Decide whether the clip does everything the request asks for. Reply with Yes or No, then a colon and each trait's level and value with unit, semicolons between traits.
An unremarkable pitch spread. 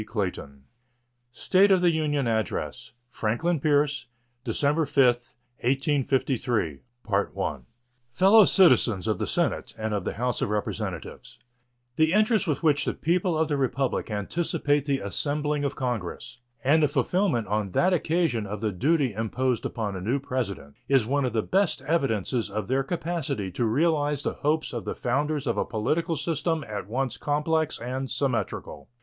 No: wide, 5.7 semitones